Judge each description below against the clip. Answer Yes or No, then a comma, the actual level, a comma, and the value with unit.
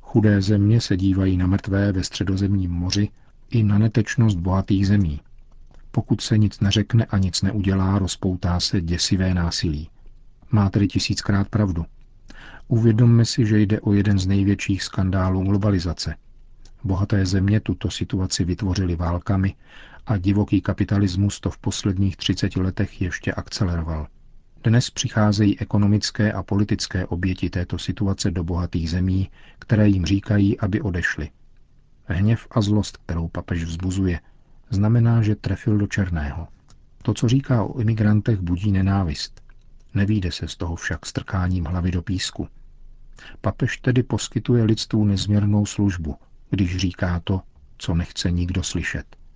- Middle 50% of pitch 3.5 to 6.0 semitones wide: No, narrow, 2.4 semitones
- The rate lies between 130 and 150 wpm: Yes, average, 135 wpm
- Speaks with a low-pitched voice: Yes, low, 100 Hz